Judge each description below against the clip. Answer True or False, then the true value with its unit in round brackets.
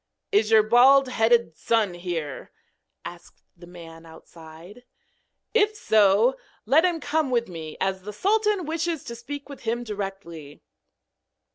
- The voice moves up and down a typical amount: False (7.7 semitones)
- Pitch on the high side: True (225 Hz)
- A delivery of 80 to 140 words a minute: True (135 wpm)